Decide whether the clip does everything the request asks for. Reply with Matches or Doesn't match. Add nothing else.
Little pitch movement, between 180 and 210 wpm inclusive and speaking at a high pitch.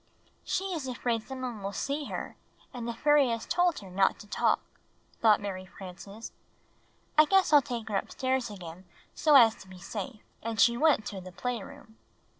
Doesn't match